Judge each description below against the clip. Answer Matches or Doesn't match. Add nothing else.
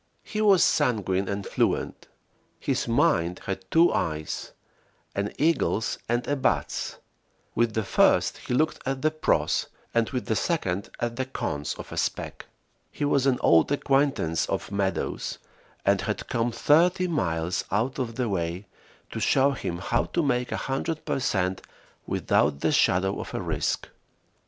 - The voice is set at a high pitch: Doesn't match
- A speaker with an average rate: Matches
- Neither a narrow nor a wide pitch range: Doesn't match